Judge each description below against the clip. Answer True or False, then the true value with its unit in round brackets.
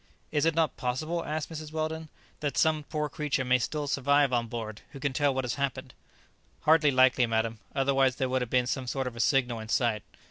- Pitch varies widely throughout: False (3.4 semitones)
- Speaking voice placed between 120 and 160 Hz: True (135 Hz)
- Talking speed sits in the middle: False (215 wpm)